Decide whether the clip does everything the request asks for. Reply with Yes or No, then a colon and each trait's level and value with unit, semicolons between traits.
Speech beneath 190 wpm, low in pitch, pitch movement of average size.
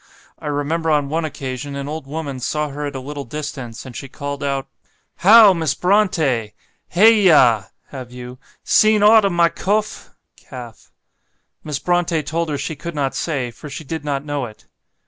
No: average, 180 wpm; medium, 145 Hz; average, 3.8 semitones